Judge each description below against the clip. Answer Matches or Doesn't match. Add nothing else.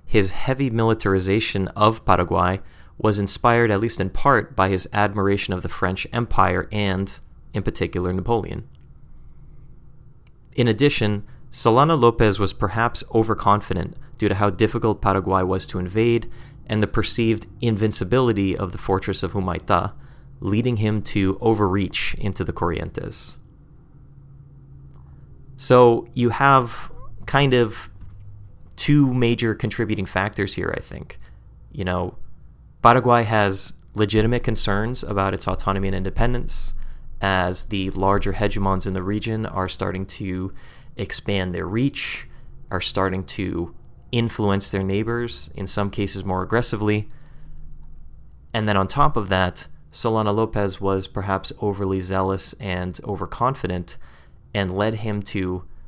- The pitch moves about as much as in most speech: Matches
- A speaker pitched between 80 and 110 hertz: Matches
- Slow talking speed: Matches